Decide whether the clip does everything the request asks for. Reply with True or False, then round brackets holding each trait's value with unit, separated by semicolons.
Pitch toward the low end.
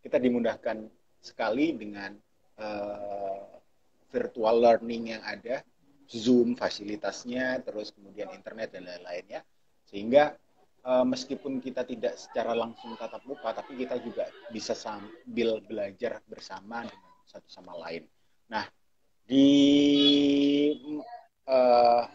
True (120 Hz)